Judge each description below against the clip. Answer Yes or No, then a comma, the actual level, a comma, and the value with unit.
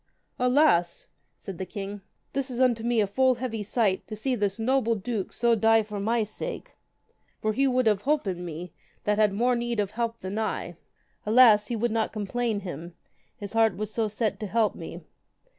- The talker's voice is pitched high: Yes, high, 220 Hz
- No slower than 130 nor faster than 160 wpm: No, average, 195 wpm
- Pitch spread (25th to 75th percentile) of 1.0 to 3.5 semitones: Yes, average, 2.8 semitones